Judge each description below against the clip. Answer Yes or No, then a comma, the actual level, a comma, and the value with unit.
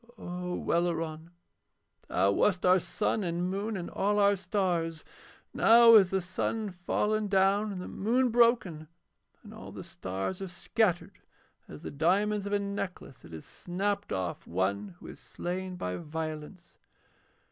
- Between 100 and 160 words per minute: Yes, average, 150 wpm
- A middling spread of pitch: Yes, average, 3.9 semitones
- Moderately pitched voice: Yes, medium, 180 Hz